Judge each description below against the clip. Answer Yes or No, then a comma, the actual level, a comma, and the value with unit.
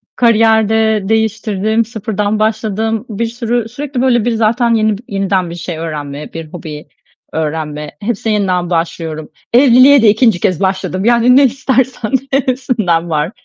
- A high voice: Yes, high, 215 Hz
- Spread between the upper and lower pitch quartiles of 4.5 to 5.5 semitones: Yes, average, 4.8 semitones